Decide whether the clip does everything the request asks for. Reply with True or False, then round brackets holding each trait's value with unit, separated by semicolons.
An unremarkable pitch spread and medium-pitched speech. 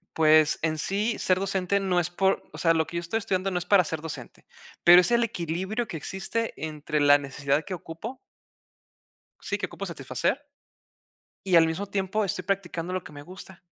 True (3.4 semitones; 180 Hz)